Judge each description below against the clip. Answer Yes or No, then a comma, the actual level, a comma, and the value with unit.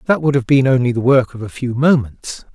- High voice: No, low, 130 Hz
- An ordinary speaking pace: No, fast, 260 wpm